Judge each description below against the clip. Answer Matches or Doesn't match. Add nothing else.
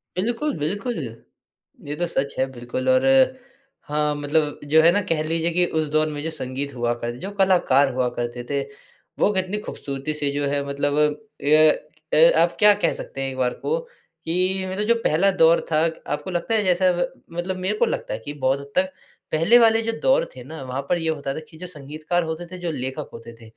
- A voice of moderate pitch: Matches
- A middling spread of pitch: Matches